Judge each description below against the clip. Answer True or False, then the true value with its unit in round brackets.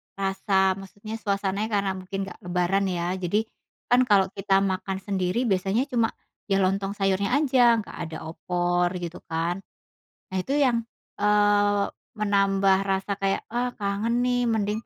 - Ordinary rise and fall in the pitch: False (2.3 semitones)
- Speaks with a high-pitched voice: True (195 Hz)